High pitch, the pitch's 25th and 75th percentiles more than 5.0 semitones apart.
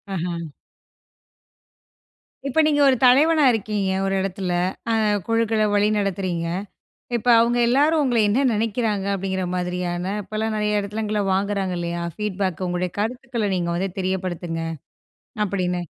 No: high, 200 Hz; average, 3.7 semitones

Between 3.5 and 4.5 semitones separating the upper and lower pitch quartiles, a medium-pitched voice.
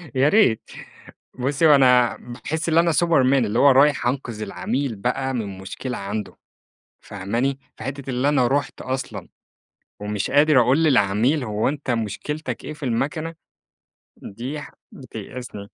No: average, 4.1 semitones; low, 130 Hz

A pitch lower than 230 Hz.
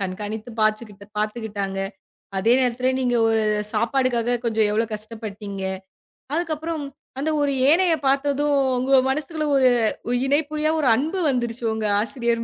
No: high, 245 Hz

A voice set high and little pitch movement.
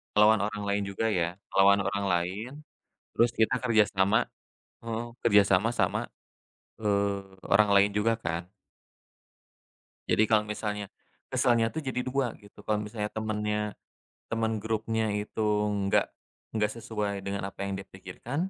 No: low, 105 Hz; narrow, 2.0 semitones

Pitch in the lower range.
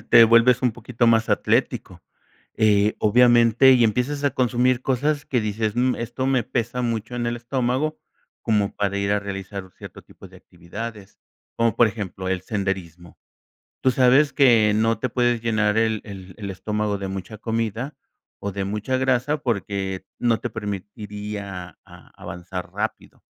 Yes: low, 110 Hz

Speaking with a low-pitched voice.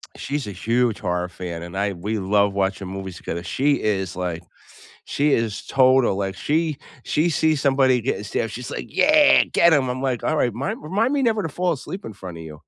Yes: low, 120 Hz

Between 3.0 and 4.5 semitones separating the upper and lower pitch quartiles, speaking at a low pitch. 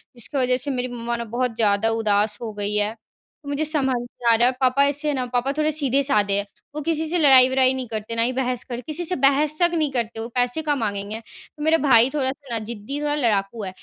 No: average, 4.1 semitones; very high, 250 Hz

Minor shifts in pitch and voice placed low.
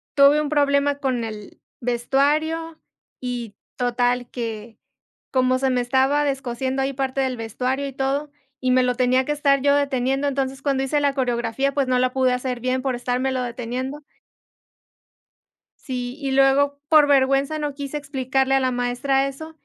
No: narrow, 2.0 semitones; very high, 265 Hz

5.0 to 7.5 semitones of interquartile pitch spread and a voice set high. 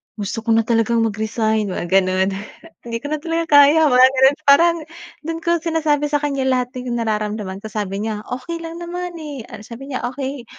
Yes: wide, 5.5 semitones; very high, 255 Hz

